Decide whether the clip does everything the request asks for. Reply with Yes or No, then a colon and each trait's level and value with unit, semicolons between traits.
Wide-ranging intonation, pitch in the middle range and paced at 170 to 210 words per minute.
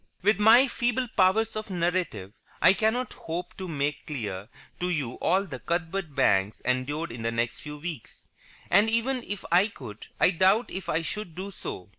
Yes: wide, 6.9 semitones; medium, 175 Hz; average, 180 wpm